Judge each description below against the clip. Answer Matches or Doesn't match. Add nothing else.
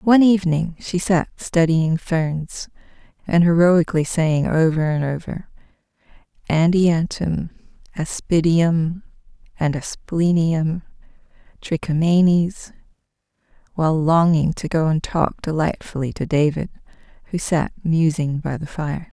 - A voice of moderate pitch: Matches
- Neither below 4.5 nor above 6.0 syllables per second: Doesn't match